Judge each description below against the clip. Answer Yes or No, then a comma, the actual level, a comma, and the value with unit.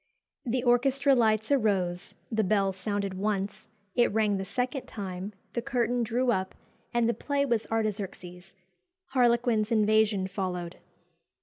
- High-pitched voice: Yes, high, 215 Hz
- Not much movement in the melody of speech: No, average, 3.7 semitones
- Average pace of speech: No, slow, 130 wpm